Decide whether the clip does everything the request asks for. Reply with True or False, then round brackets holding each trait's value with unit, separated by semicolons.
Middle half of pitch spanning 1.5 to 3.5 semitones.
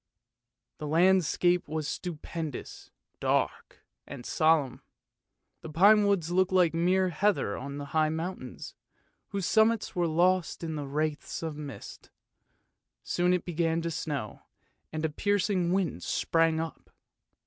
True (2.9 semitones)